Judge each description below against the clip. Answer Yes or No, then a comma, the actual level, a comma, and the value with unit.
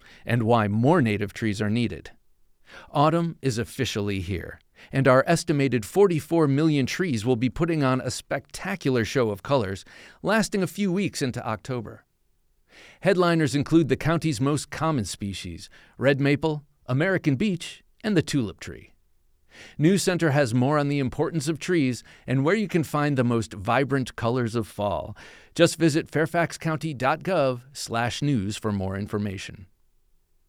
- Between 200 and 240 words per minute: No, average, 145 wpm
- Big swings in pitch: Yes, wide, 6.4 semitones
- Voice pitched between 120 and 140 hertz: Yes, low, 135 Hz